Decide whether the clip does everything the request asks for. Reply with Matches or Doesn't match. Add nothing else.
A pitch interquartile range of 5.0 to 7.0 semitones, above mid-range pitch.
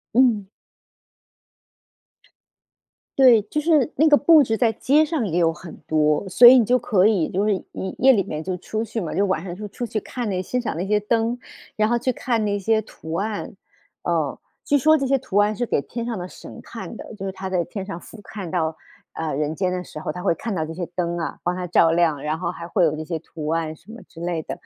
Matches